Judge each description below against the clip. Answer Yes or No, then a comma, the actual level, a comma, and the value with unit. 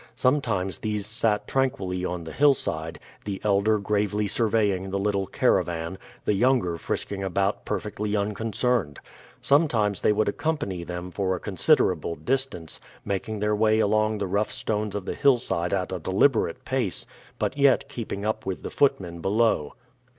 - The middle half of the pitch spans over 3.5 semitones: No, average, 3.2 semitones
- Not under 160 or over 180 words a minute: No, average, 150 wpm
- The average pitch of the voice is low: Yes, low, 105 Hz